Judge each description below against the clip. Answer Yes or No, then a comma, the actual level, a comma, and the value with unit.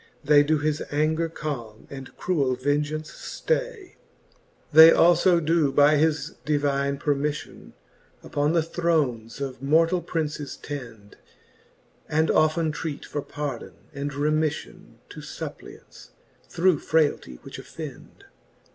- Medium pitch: Yes, medium, 150 Hz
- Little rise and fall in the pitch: Yes, narrow, 2.3 semitones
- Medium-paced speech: No, slow, 120 wpm